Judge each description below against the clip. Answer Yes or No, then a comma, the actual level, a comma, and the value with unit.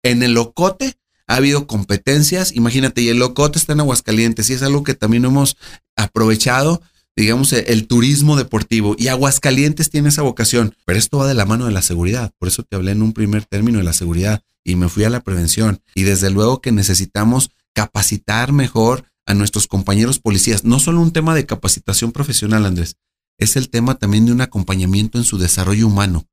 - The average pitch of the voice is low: Yes, low, 115 Hz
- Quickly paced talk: Yes, fast, 195 wpm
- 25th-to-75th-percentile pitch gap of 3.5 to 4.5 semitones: Yes, average, 4.2 semitones